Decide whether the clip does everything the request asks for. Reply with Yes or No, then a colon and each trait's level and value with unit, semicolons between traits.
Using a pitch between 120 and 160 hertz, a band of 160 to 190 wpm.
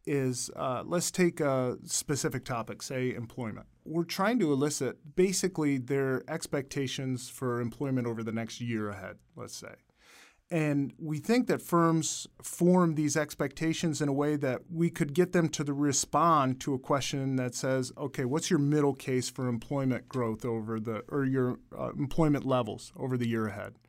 Yes: medium, 140 Hz; average, 170 wpm